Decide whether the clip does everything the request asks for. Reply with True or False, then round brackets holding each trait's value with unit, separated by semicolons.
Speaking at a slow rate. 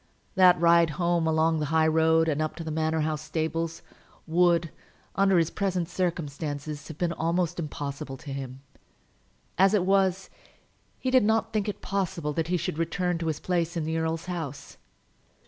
False (175 wpm)